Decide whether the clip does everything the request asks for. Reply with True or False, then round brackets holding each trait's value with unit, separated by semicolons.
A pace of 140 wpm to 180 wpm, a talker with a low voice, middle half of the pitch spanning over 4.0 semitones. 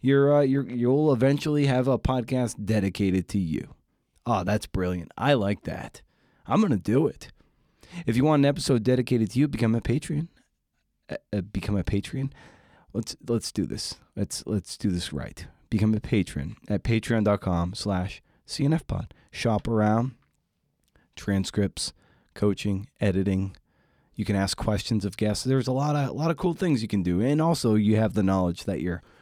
True (170 wpm; 110 Hz; 5.1 semitones)